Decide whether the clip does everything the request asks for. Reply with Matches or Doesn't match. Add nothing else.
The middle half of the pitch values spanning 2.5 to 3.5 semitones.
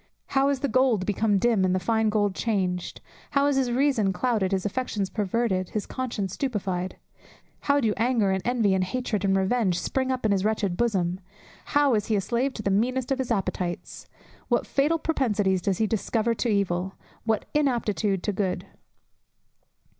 Doesn't match